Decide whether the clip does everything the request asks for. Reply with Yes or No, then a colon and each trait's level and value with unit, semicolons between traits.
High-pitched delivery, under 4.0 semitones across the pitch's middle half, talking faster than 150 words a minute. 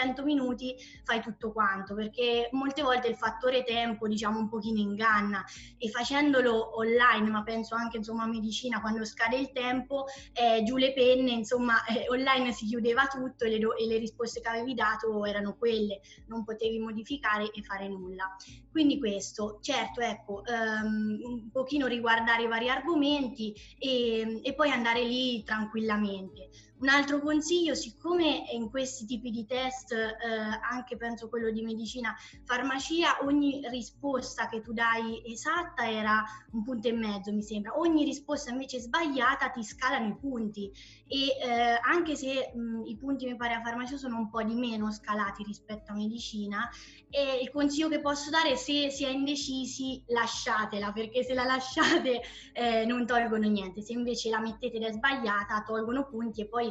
Yes: high, 235 Hz; average, 2.9 semitones; average, 165 wpm